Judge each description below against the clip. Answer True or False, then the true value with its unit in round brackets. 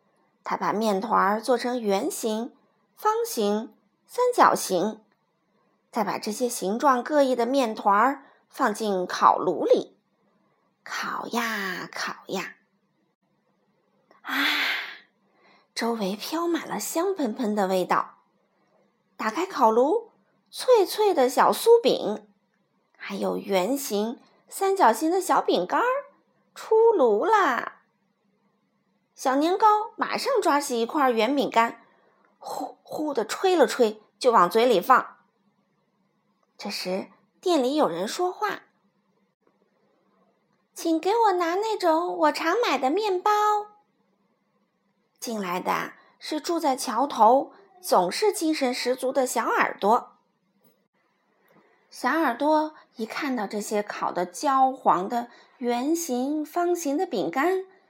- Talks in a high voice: True (265 Hz)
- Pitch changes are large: True (8.4 semitones)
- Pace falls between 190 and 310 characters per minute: False (160 characters per minute)